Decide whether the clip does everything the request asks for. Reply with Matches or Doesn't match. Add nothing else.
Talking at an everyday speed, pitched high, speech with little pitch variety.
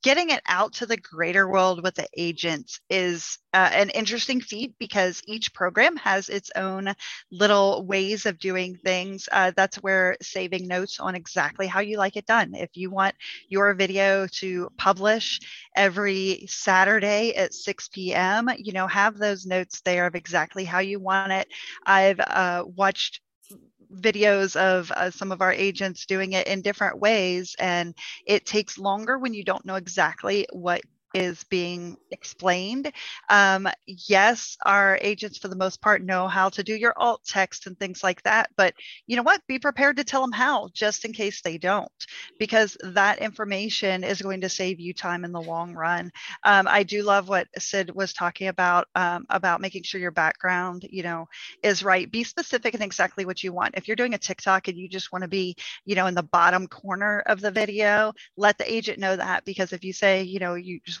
Matches